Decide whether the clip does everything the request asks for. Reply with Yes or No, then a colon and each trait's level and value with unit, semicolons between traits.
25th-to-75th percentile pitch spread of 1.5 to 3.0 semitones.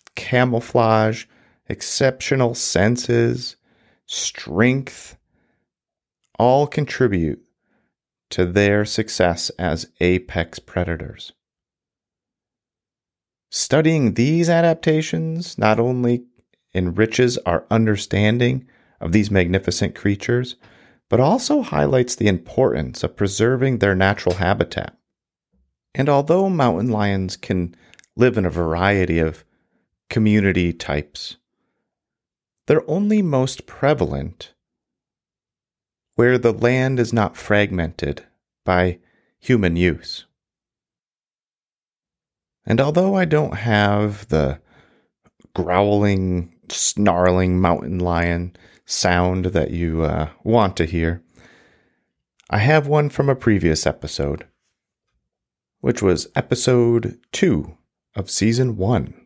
No: wide, 5.5 semitones